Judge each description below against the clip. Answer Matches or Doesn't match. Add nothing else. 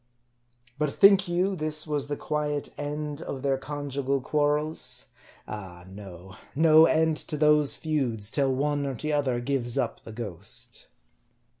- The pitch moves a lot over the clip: Doesn't match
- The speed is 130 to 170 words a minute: Matches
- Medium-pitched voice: Matches